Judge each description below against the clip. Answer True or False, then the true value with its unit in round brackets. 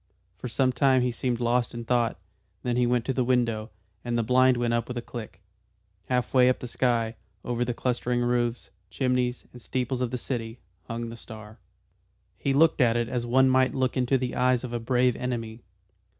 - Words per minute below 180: False (205 wpm)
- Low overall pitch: True (125 Hz)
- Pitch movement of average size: False (1.4 semitones)